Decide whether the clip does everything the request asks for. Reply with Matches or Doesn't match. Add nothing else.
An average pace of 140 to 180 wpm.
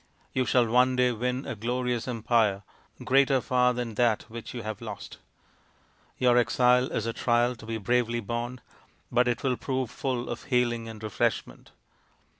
Matches